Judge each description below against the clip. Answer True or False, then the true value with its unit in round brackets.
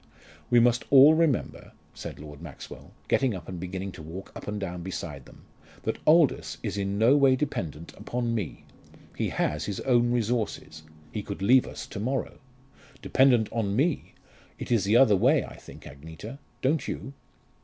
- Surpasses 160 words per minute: True (175 wpm)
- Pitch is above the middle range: False (110 Hz)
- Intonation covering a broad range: True (6.0 semitones)